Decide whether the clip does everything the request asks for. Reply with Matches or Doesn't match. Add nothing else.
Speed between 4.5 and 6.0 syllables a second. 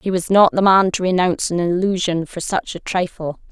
Matches